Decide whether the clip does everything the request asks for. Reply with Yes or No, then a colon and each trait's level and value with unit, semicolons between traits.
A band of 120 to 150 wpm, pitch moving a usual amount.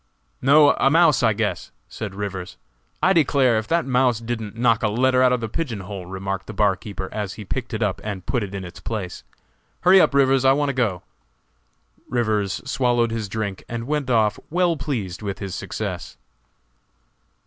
No: average, 185 wpm; average, 4.4 semitones